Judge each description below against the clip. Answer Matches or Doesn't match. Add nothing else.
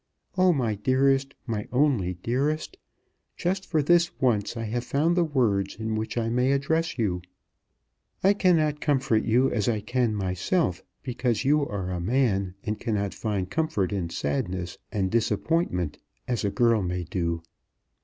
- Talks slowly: Doesn't match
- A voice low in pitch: Matches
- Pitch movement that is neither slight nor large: Doesn't match